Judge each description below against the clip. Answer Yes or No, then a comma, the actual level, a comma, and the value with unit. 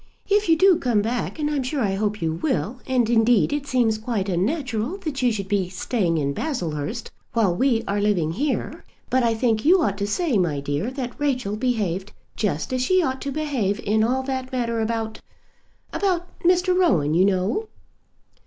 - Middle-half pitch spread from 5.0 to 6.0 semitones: Yes, wide, 5.4 semitones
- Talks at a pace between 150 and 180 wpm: No, average, 190 wpm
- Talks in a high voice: Yes, high, 235 Hz